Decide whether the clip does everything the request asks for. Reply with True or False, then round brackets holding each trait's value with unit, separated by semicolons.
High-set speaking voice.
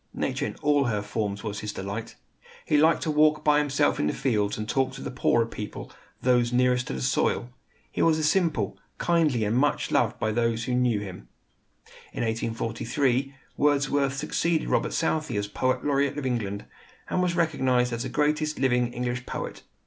False (125 Hz)